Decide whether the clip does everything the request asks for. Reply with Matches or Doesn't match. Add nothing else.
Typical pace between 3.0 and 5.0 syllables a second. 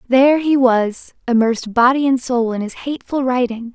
Doesn't match